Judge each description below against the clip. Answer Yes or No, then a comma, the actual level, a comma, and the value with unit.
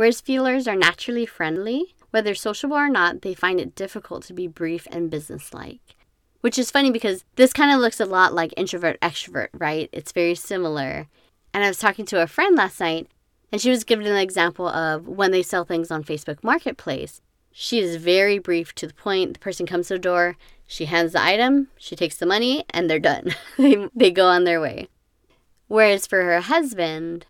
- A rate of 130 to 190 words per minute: No, average, 200 wpm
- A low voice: No, medium, 185 Hz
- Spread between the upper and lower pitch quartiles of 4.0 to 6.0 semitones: Yes, average, 5.0 semitones